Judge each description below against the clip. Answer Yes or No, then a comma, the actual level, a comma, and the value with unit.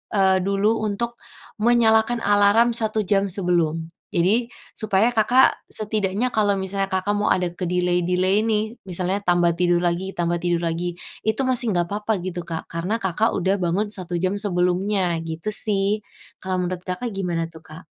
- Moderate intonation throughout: Yes, average, 3.2 semitones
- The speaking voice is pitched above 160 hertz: Yes, high, 190 Hz